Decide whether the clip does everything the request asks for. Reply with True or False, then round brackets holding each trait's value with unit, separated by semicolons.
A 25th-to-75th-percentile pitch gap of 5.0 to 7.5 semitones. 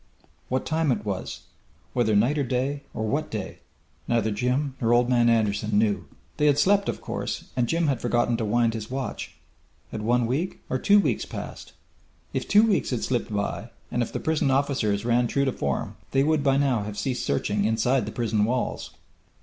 False (4.0 semitones)